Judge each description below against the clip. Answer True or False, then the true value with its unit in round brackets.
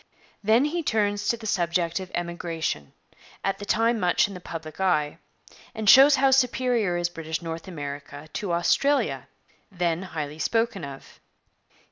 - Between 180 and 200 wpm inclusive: False (150 wpm)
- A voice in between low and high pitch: True (180 Hz)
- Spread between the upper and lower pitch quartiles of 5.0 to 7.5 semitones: True (5.3 semitones)